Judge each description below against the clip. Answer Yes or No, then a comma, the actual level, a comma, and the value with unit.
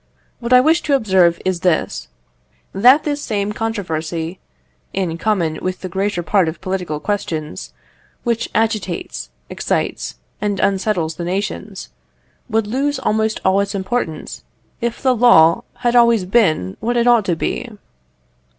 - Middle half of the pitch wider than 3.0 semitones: Yes, average, 5.1 semitones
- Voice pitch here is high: Yes, high, 200 Hz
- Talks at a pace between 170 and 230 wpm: No, average, 140 wpm